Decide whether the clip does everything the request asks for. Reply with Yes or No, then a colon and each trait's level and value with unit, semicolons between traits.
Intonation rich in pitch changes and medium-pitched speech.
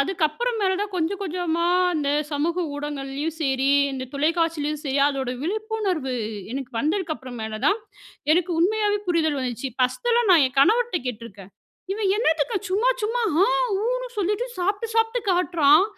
No: wide, 6.8 semitones; very high, 330 Hz